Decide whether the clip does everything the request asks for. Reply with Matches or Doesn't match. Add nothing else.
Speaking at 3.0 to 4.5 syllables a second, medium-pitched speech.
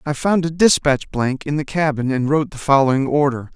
Doesn't match